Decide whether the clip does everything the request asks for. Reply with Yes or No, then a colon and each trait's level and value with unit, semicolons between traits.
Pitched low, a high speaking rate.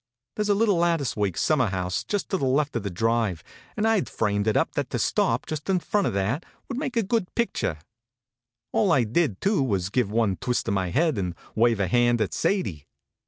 Yes: low, 120 Hz; fast, 245 wpm